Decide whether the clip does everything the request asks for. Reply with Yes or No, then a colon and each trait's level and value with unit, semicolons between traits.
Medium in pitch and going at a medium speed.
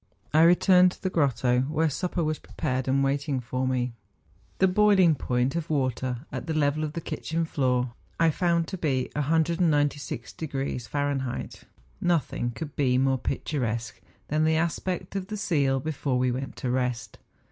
Yes: medium, 145 Hz; average, 170 wpm